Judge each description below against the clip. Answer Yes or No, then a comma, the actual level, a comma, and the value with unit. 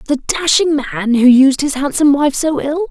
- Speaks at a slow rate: No, fast, 205 wpm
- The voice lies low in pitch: No, very high, 285 Hz